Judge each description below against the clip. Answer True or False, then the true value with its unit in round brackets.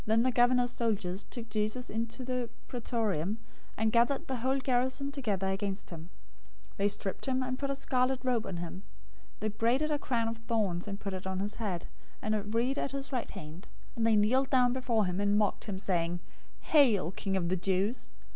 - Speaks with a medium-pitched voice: False (225 Hz)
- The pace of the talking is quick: True (210 wpm)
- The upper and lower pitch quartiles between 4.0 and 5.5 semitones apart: True (4.5 semitones)